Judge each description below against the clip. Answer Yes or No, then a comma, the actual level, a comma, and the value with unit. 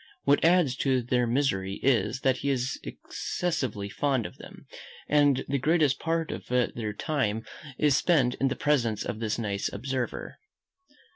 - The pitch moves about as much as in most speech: Yes, average, 3.8 semitones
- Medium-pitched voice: No, low, 130 Hz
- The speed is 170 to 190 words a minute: No, average, 155 wpm